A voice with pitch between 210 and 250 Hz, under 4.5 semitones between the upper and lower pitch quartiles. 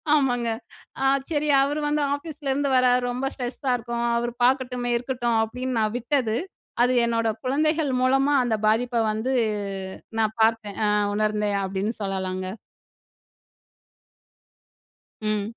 Yes: high, 245 Hz; average, 3.5 semitones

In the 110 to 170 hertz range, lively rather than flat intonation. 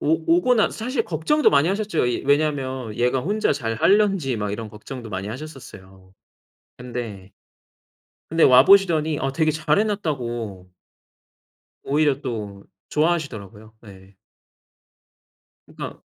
Yes: low, 135 Hz; wide, 6.7 semitones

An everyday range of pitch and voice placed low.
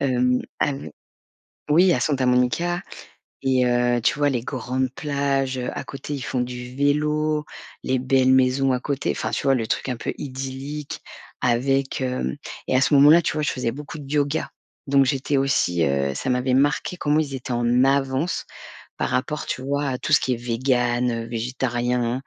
No: narrow, 2.3 semitones; low, 130 Hz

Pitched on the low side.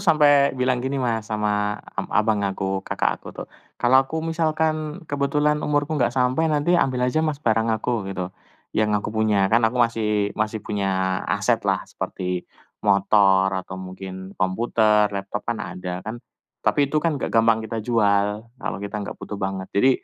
Yes: low, 110 Hz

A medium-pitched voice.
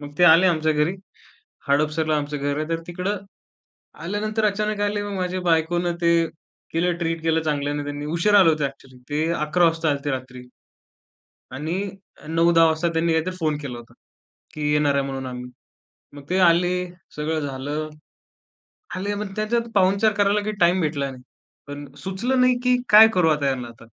Yes: medium, 160 Hz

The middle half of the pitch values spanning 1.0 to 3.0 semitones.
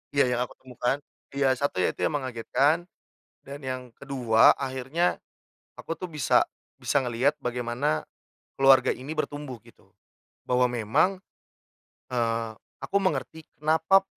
No: average, 3.5 semitones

